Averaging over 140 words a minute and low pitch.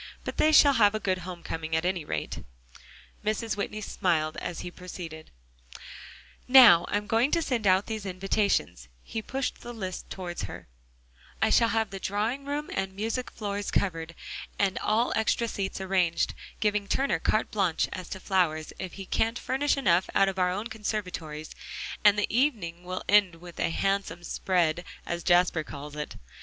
No: average, 175 wpm; high, 195 Hz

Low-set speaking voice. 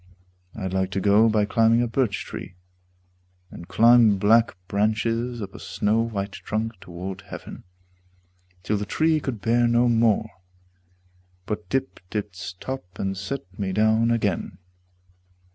Yes: low, 110 Hz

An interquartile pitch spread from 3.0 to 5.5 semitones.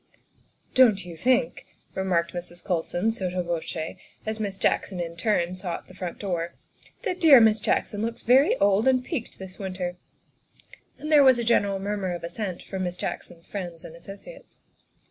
Yes: average, 4.1 semitones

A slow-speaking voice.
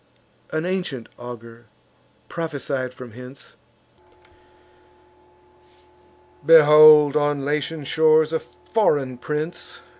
Yes: slow, 80 wpm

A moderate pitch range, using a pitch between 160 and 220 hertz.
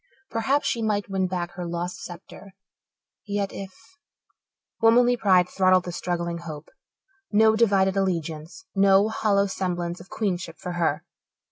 Yes: average, 3.0 semitones; high, 190 Hz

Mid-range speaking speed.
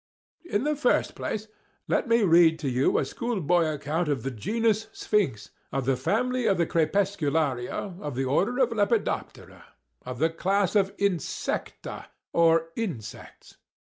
No: slow, 130 wpm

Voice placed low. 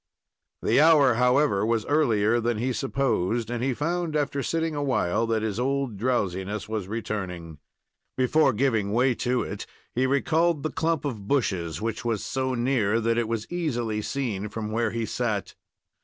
Yes: low, 120 Hz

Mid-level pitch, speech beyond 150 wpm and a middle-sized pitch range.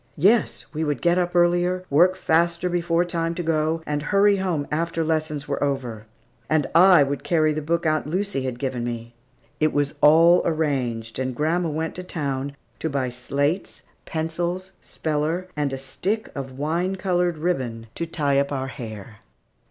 Yes: medium, 155 Hz; average, 170 wpm; average, 3.8 semitones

